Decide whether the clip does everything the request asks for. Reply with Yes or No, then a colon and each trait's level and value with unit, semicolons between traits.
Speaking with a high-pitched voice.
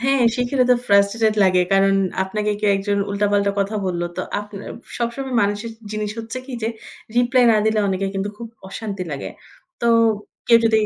Yes: high, 210 Hz